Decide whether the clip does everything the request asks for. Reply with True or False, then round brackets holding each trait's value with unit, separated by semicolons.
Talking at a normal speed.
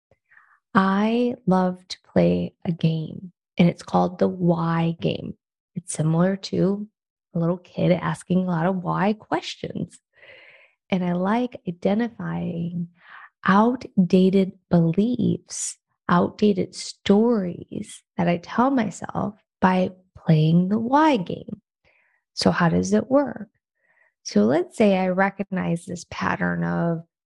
False (120 wpm)